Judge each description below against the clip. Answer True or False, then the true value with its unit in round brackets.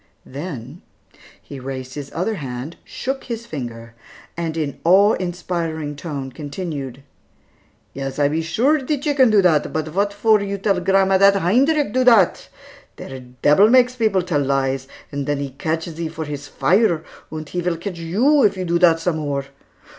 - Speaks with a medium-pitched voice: True (170 Hz)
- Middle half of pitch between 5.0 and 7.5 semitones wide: True (5.6 semitones)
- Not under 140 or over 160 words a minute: False (175 wpm)